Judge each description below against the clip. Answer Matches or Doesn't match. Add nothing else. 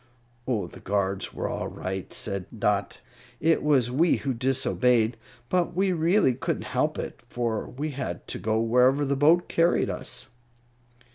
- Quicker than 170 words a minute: Doesn't match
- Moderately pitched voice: Doesn't match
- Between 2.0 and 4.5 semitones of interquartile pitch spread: Doesn't match